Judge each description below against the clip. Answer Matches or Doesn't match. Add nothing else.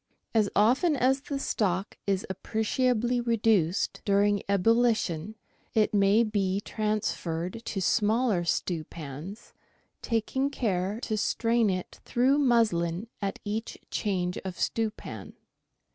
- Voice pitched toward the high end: Matches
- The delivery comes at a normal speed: Doesn't match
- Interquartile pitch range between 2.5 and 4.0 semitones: Matches